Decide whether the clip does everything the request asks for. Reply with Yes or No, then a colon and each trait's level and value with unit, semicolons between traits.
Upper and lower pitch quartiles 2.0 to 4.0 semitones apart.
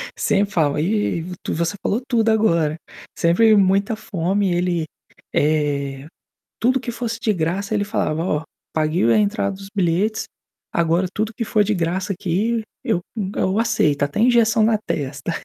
No: average, 4.9 semitones